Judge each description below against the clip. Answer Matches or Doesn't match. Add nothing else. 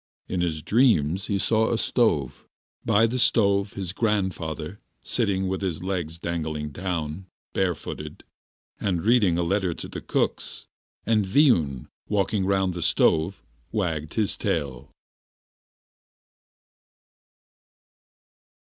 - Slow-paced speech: Matches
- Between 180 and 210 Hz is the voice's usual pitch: Doesn't match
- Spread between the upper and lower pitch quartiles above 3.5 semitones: Matches